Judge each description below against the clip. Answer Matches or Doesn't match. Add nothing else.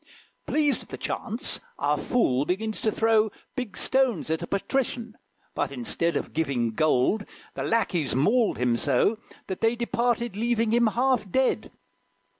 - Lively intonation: Matches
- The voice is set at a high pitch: Matches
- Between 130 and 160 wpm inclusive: Matches